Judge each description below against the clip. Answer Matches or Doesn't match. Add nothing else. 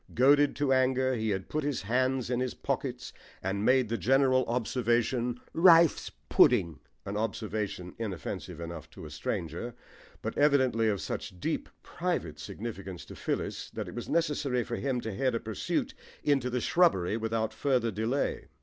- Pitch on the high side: Doesn't match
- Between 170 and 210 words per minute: Doesn't match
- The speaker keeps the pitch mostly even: Doesn't match